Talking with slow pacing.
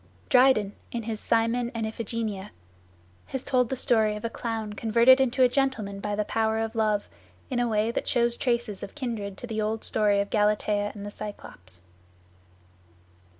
No: average, 175 wpm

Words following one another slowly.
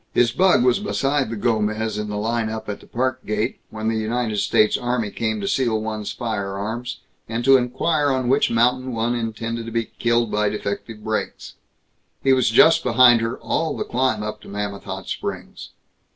No: average, 190 wpm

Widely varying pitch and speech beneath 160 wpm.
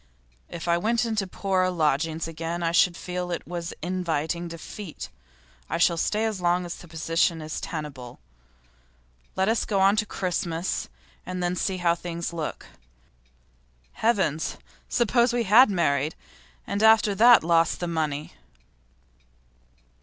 No: average, 3.1 semitones; average, 140 wpm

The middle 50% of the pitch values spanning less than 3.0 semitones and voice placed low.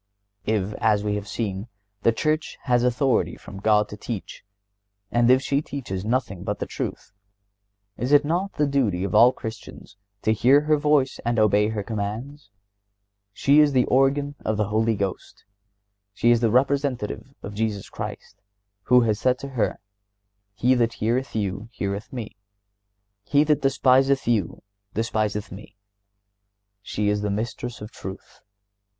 No: average, 4.3 semitones; low, 115 Hz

